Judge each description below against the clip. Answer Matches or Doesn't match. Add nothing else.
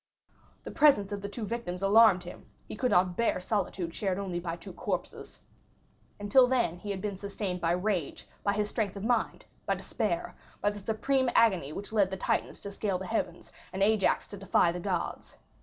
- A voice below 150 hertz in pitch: Doesn't match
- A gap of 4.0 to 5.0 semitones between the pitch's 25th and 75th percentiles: Doesn't match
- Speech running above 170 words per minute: Matches